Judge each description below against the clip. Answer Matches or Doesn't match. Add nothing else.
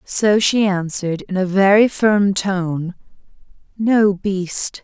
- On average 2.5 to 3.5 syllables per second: Matches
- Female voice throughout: Matches